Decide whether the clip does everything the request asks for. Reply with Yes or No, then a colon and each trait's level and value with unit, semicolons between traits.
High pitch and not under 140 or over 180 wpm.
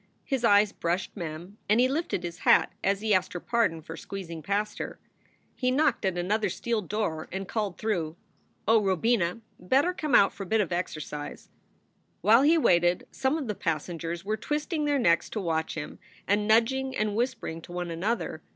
No: high, 205 Hz; average, 190 wpm